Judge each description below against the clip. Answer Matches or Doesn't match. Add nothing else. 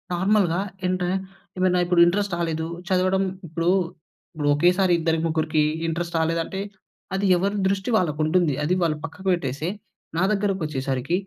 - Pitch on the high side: Doesn't match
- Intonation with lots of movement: Doesn't match